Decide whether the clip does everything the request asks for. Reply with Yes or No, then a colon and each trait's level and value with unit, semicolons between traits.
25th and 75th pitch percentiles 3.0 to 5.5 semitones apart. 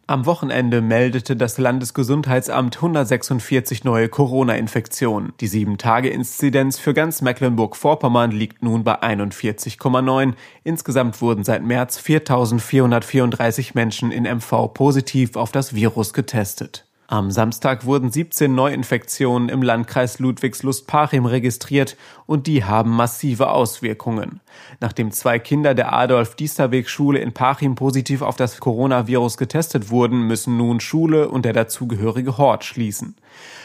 No: narrow, 2.6 semitones